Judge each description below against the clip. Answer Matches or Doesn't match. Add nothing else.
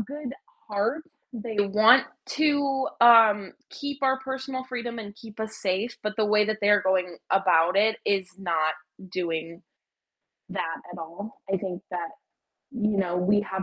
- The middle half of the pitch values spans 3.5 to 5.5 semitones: Matches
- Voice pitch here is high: Matches